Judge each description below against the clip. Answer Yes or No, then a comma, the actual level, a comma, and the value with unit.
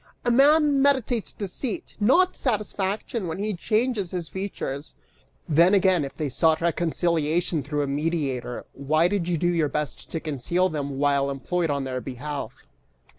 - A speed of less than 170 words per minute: Yes, average, 155 wpm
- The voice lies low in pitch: No, medium, 170 Hz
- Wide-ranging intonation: Yes, wide, 5.9 semitones